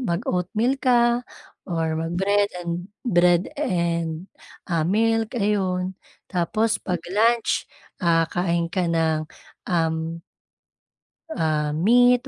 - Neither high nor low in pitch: Yes, medium, 180 Hz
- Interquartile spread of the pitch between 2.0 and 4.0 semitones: No, average, 4.6 semitones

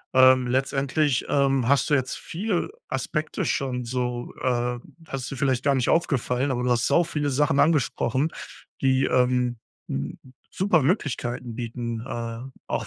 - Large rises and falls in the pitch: No, narrow, 2.5 semitones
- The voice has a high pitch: No, low, 130 Hz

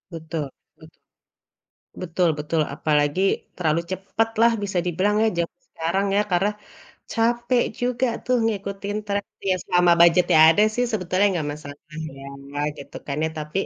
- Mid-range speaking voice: Yes, medium, 180 Hz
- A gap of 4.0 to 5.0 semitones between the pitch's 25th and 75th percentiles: Yes, average, 4.4 semitones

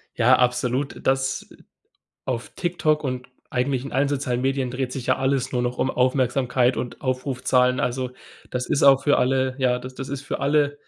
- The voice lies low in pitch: Yes, low, 130 Hz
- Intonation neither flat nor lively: No, narrow, 1.4 semitones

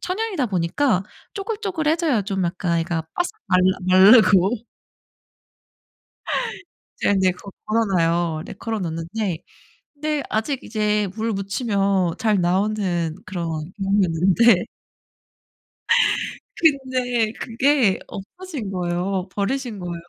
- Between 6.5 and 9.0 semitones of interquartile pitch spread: No, wide, 5.6 semitones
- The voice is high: Yes, high, 200 Hz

